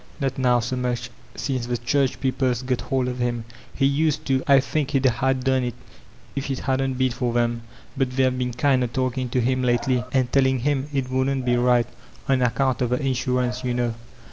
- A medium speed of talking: No, fast, 210 wpm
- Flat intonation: Yes, narrow, 1.4 semitones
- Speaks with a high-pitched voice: No, low, 130 Hz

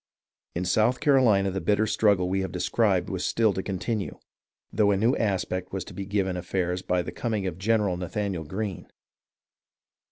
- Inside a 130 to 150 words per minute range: No, average, 170 wpm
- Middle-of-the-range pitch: No, low, 100 Hz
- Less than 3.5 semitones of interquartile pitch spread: Yes, average, 2.7 semitones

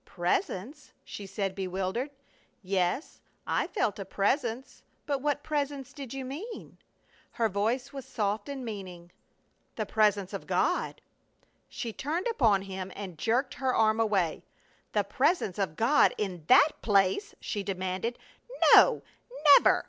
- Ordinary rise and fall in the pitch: No, wide, 5.8 semitones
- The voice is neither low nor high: No, high, 215 Hz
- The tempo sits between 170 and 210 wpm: No, slow, 135 wpm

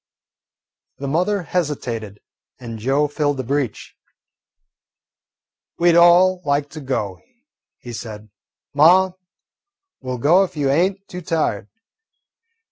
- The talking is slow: Yes, slow, 120 wpm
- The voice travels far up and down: Yes, wide, 5.7 semitones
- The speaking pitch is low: No, medium, 145 Hz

